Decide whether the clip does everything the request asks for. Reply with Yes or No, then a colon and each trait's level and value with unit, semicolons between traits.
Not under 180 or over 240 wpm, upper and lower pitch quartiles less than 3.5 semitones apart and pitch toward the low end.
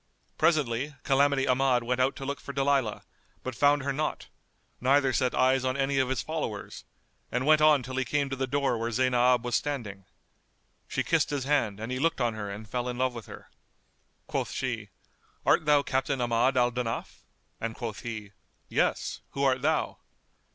Yes: average, 185 wpm; average, 2.7 semitones; low, 130 Hz